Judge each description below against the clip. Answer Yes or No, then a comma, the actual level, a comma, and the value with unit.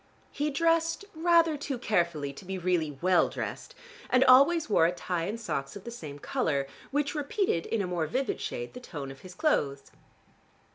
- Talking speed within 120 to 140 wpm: No, average, 185 wpm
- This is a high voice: Yes, high, 200 Hz